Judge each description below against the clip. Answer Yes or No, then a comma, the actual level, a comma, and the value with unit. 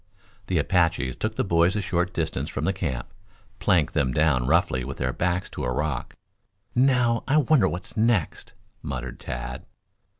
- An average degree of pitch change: No, wide, 6.3 semitones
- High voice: No, very low, 85 Hz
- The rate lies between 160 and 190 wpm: Yes, average, 165 wpm